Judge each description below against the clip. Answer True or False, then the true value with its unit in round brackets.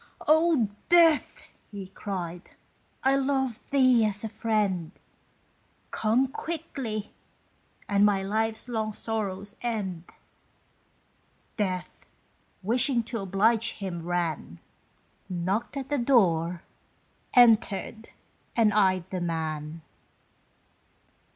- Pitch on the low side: False (215 Hz)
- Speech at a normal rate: False (95 wpm)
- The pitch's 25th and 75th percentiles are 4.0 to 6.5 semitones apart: True (4.5 semitones)